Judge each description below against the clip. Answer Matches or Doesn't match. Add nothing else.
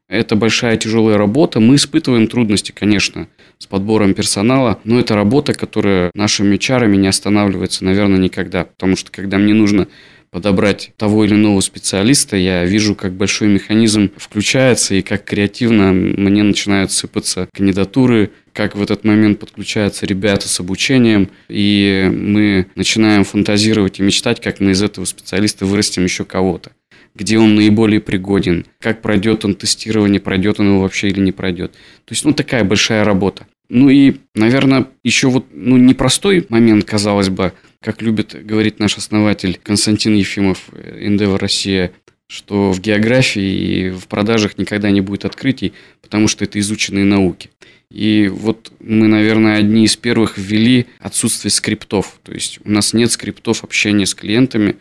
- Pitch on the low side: Matches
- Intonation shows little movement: Matches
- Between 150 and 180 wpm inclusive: Matches